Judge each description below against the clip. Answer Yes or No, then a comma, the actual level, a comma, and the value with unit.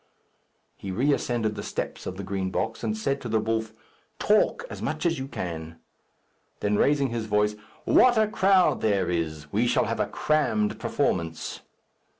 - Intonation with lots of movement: Yes, wide, 6.8 semitones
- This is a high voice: No, low, 110 Hz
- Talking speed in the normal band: Yes, average, 170 wpm